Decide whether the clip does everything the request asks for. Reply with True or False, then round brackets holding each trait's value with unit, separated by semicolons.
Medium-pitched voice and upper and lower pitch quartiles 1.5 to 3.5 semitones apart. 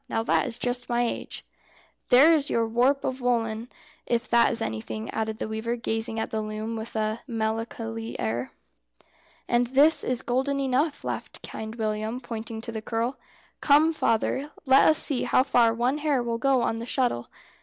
False (235 Hz; 2.6 semitones)